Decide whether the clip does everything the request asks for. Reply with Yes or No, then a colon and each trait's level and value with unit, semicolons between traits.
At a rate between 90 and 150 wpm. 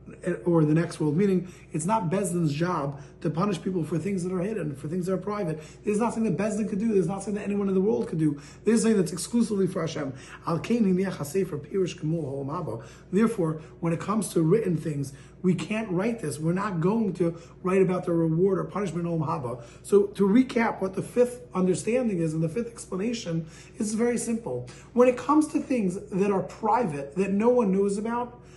No: average, 195 wpm